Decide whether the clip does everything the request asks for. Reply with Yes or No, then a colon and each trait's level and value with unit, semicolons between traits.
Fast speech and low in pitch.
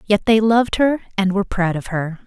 No: fast, 240 wpm; high, 205 Hz